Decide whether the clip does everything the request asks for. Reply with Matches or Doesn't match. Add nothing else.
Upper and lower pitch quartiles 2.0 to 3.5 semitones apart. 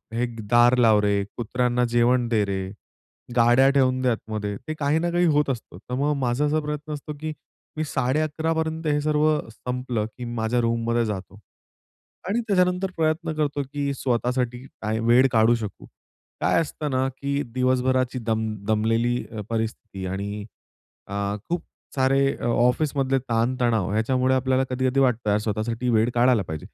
Doesn't match